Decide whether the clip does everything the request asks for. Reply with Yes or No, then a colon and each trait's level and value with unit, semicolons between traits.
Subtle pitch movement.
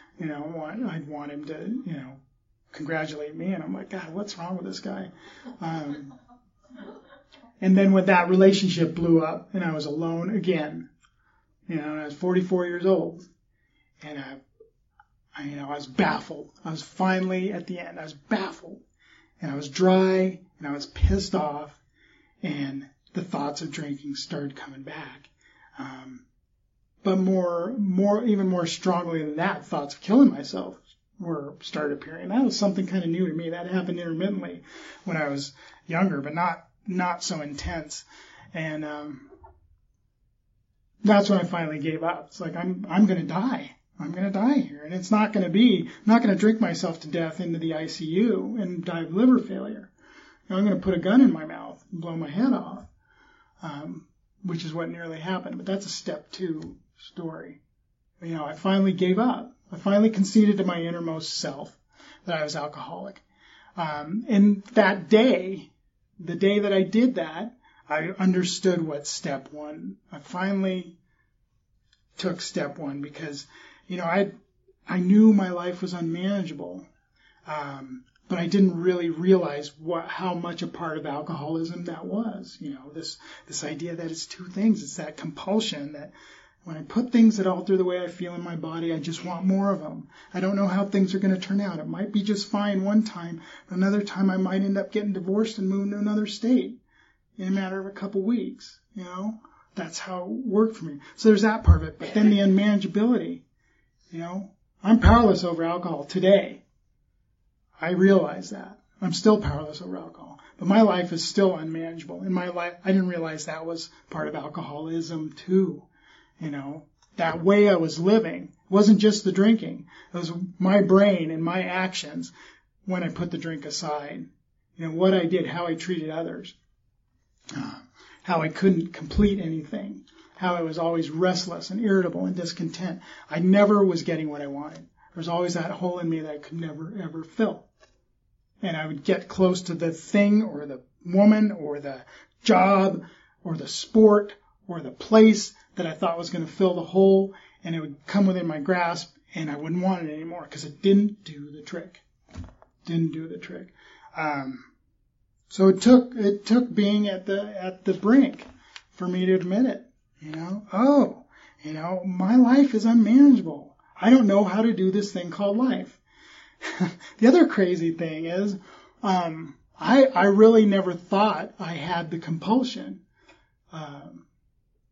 No: average, 4.0 semitones